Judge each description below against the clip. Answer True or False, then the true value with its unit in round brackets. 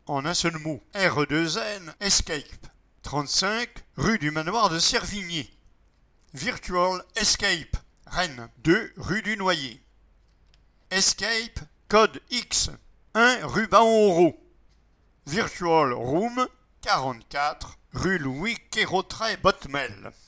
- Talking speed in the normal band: False (95 wpm)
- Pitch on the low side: False (175 Hz)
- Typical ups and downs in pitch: False (6.9 semitones)